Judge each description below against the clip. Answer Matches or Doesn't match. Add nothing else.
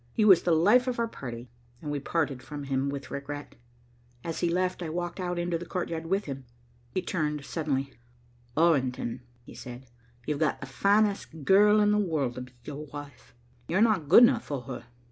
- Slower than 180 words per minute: Doesn't match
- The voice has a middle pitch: Matches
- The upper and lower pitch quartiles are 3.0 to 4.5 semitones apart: Doesn't match